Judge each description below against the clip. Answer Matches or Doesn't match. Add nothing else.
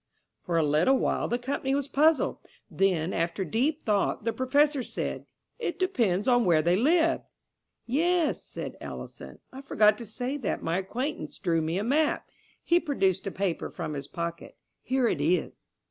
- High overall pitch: Matches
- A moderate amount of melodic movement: Doesn't match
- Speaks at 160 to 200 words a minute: Matches